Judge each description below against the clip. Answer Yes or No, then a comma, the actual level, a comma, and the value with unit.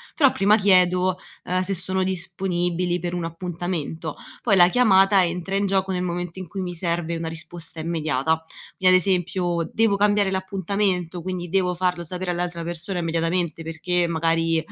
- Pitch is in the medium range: Yes, medium, 180 Hz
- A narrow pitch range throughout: Yes, narrow, 2.0 semitones